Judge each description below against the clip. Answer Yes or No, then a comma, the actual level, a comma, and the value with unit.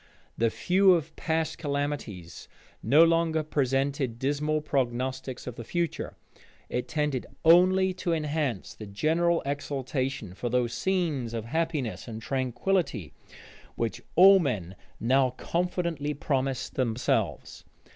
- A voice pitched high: No, medium, 140 Hz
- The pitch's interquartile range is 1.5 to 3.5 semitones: No, average, 5.0 semitones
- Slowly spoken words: Yes, slow, 115 wpm